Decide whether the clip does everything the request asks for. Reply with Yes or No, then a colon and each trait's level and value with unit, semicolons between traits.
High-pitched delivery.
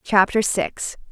Yes: high, 205 Hz